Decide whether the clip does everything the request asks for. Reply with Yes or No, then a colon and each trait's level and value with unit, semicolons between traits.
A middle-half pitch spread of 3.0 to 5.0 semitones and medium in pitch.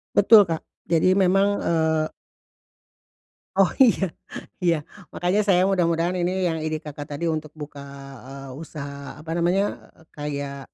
Yes: average, 3.5 semitones; medium, 165 Hz